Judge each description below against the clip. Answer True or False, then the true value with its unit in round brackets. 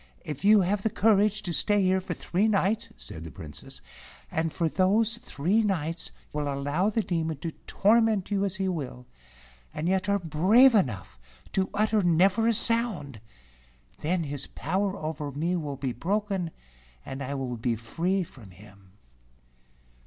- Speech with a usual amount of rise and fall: False (6.1 semitones)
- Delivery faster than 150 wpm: True (160 wpm)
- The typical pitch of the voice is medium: True (180 Hz)